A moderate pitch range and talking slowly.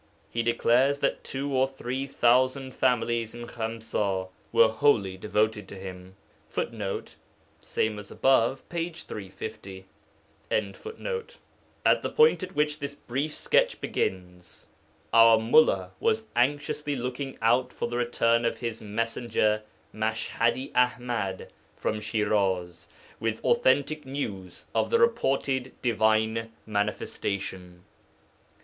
Yes: average, 4.1 semitones; slow, 110 wpm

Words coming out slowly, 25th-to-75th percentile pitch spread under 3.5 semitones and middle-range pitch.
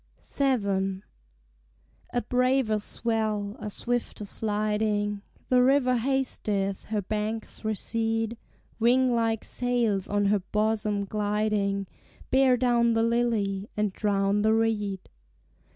No: slow, 105 wpm; narrow, 2.4 semitones; high, 215 Hz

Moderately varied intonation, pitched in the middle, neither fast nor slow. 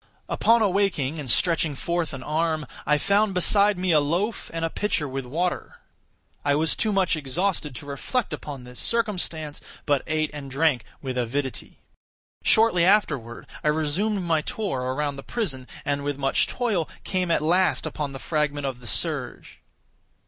Yes: average, 4.8 semitones; medium, 155 Hz; average, 165 wpm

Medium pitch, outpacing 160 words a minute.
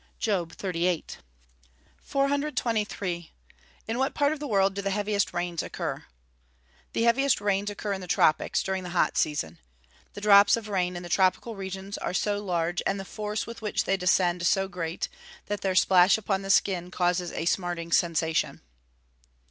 No: high, 195 Hz; average, 170 wpm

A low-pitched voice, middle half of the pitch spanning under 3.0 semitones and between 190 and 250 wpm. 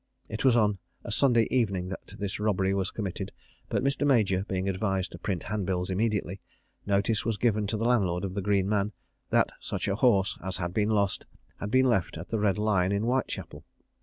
Yes: low, 100 Hz; narrow, 2.5 semitones; fast, 205 wpm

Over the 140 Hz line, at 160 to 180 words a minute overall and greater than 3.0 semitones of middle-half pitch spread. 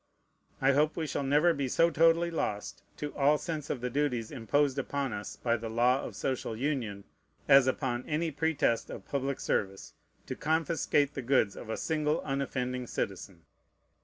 No: low, 135 Hz; average, 170 wpm; average, 3.8 semitones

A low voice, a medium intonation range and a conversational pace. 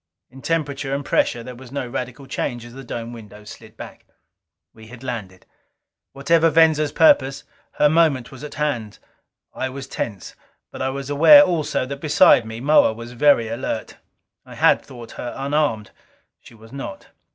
Yes: low, 130 Hz; average, 4.0 semitones; average, 170 wpm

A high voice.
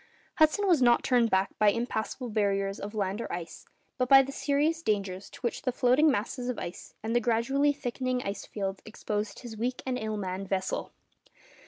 Yes: high, 230 Hz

